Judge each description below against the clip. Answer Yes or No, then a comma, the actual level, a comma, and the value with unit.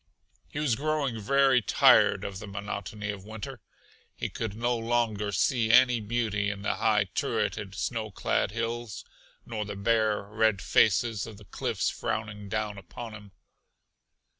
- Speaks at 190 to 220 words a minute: No, average, 150 wpm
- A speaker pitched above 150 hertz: No, low, 110 Hz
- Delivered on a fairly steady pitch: Yes, narrow, 2.3 semitones